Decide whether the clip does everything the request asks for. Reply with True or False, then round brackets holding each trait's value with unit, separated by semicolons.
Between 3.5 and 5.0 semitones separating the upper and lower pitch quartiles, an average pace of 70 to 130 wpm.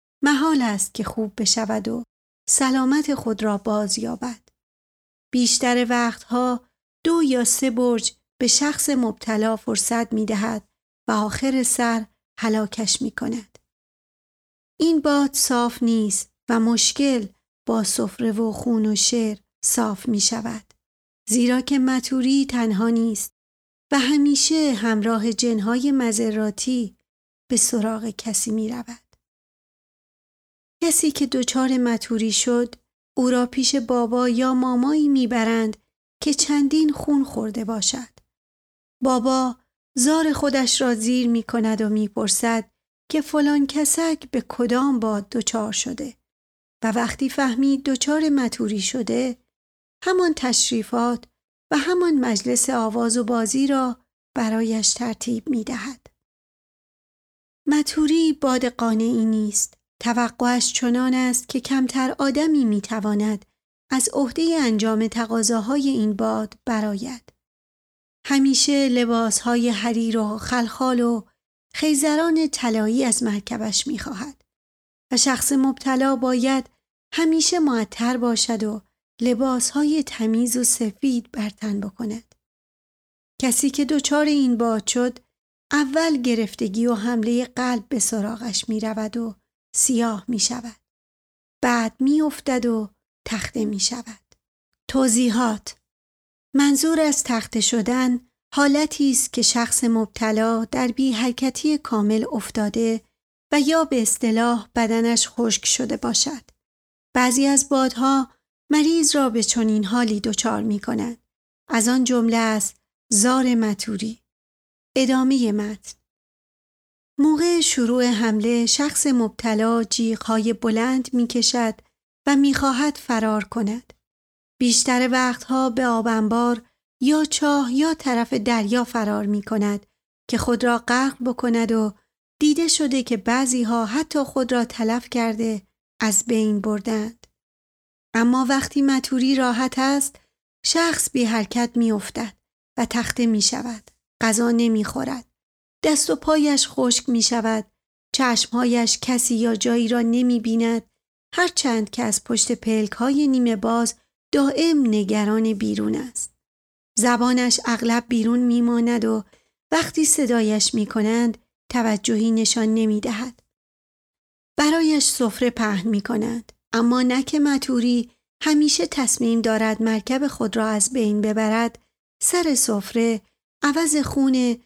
False (2.9 semitones; 120 wpm)